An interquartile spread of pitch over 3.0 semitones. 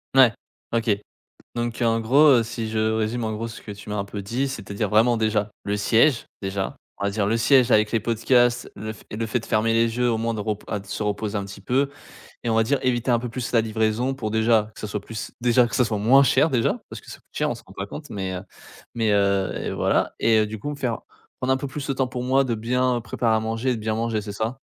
No: narrow, 2.4 semitones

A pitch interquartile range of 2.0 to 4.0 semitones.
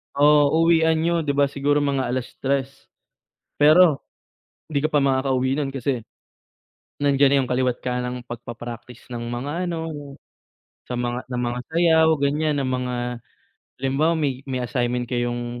Yes: average, 3.0 semitones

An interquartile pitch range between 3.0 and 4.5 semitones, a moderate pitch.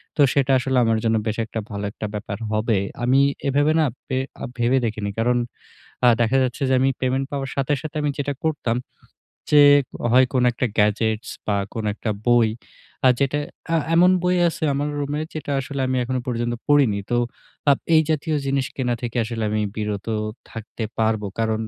No: average, 3.8 semitones; low, 125 Hz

